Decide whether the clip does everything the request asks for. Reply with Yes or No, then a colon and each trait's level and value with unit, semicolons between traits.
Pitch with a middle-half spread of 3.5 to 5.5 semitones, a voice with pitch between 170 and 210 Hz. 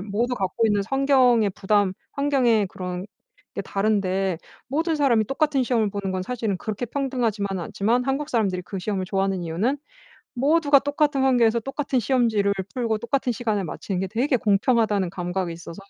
No: average, 5.1 semitones; high, 220 Hz